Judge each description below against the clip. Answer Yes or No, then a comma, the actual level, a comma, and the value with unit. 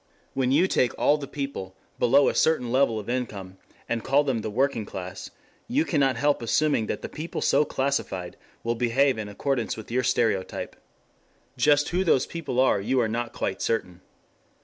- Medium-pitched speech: No, low, 125 Hz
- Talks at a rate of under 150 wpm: No, average, 180 wpm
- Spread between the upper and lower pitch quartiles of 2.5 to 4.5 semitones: Yes, average, 4.2 semitones